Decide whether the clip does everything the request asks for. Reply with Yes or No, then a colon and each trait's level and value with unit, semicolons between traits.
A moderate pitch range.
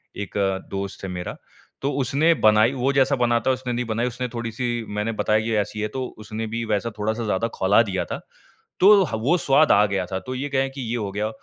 Yes: average, 3.6 semitones